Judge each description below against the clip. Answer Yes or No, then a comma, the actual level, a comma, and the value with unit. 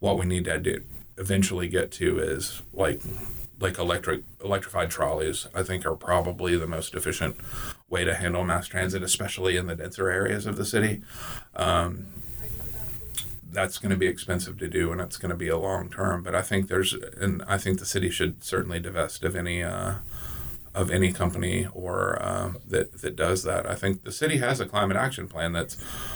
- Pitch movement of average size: No, narrow, 1.8 semitones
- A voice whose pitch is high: No, very low, 95 Hz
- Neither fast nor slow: Yes, average, 190 wpm